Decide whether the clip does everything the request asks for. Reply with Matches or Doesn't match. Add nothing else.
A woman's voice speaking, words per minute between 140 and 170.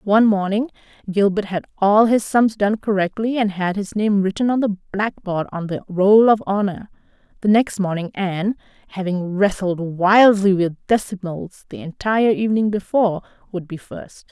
Matches